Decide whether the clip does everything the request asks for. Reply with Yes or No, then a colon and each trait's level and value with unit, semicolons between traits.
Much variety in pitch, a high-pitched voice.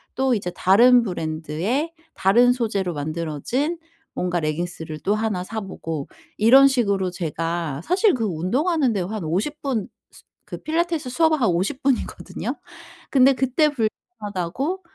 Yes: wide, 7.4 semitones; high, 215 Hz